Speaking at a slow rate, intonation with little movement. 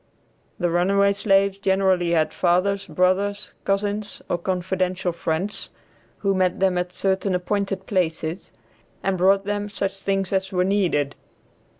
Yes: slow, 130 wpm; narrow, 1.7 semitones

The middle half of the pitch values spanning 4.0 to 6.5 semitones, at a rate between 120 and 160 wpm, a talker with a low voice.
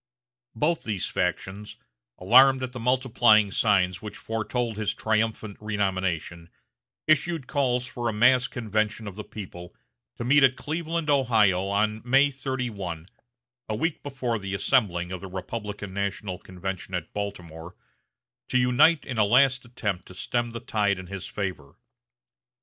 Yes: average, 4.6 semitones; average, 145 wpm; low, 110 Hz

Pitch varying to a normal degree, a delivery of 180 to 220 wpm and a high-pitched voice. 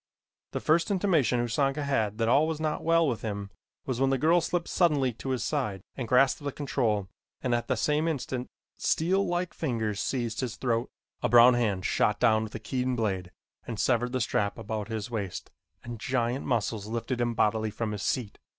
No: average, 4.1 semitones; average, 195 wpm; low, 120 Hz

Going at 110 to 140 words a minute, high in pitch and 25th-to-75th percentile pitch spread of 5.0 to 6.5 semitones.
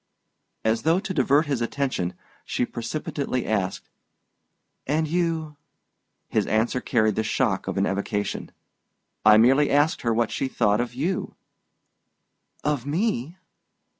No: slow, 135 wpm; low, 130 Hz; wide, 5.4 semitones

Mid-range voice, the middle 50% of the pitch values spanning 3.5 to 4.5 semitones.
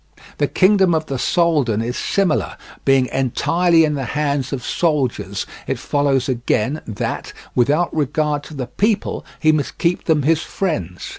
Yes: medium, 150 Hz; average, 4.1 semitones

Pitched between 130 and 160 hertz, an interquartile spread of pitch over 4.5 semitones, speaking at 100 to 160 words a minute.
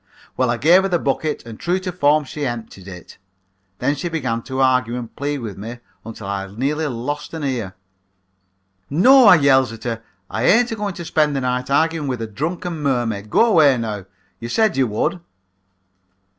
No: low, 135 Hz; wide, 5.6 semitones; average, 190 wpm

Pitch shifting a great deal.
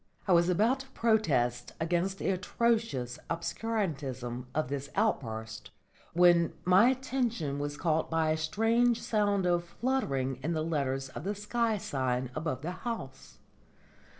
Yes: wide, 7.9 semitones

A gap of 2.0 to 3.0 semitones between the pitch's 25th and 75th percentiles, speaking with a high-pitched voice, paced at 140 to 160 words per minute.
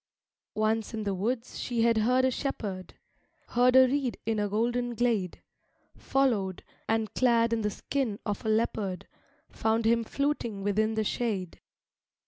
Yes: average, 2.7 semitones; high, 225 Hz; average, 155 wpm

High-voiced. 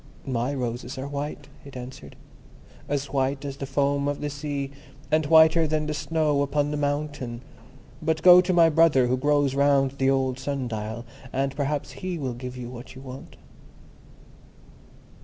No: medium, 140 Hz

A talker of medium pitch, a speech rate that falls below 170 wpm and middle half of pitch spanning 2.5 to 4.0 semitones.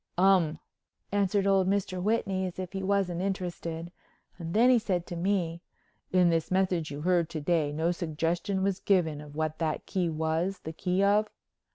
No: medium, 180 Hz; average, 180 wpm; average, 2.9 semitones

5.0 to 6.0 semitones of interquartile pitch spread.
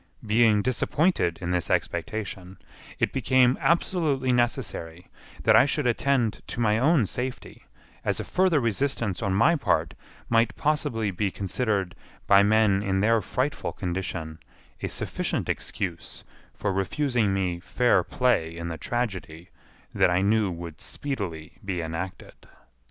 Yes: wide, 5.6 semitones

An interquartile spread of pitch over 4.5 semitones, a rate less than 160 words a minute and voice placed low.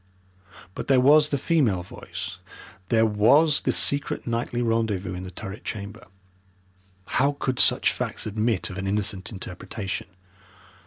Yes: average, 5.1 semitones; average, 140 wpm; low, 110 Hz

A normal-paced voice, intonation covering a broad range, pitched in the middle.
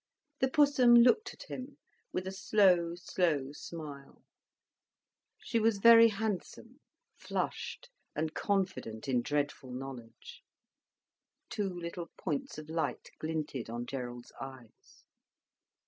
No: slow, 110 wpm; wide, 7.9 semitones; medium, 170 Hz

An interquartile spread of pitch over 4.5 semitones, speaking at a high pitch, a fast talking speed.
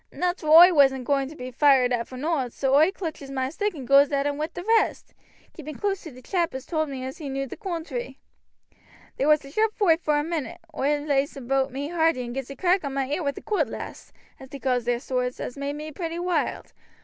No: average, 3.5 semitones; very high, 285 Hz; fast, 245 wpm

